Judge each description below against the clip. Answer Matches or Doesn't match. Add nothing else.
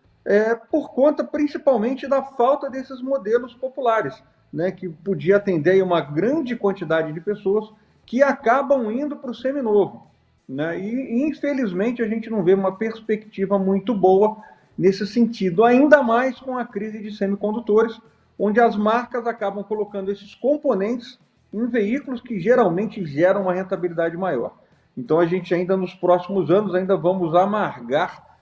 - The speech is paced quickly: Doesn't match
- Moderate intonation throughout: Matches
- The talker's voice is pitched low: Doesn't match